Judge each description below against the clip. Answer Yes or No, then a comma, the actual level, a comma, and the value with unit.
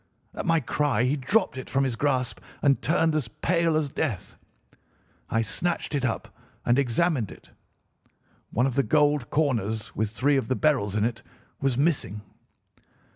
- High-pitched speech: No, low, 135 Hz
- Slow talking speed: No, average, 165 wpm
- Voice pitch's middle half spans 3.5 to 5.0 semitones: Yes, average, 4.6 semitones